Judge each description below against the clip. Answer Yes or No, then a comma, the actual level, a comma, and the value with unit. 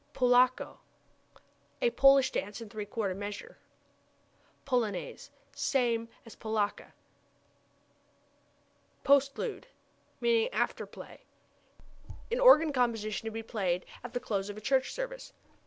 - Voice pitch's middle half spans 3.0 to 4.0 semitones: No, average, 4.5 semitones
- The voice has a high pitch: Yes, high, 240 Hz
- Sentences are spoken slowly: Yes, slow, 110 wpm